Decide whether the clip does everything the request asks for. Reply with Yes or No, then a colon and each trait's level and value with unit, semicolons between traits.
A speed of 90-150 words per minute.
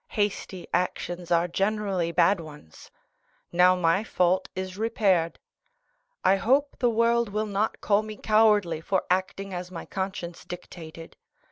Yes: slow, 135 wpm